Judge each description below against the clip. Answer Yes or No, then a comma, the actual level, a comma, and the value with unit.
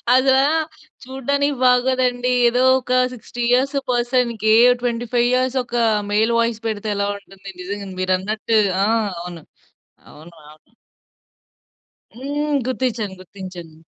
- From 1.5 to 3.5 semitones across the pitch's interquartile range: No, average, 4.1 semitones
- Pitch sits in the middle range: No, high, 235 Hz